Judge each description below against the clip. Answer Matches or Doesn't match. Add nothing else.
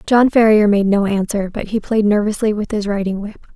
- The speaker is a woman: Matches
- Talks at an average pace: Doesn't match